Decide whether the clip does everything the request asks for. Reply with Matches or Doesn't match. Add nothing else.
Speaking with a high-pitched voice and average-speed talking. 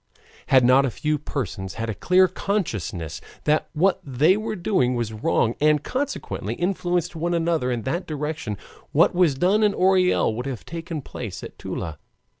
Doesn't match